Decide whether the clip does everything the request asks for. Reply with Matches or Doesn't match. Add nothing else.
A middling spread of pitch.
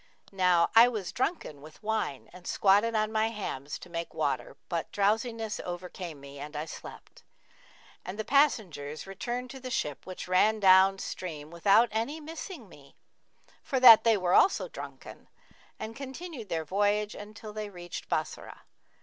Matches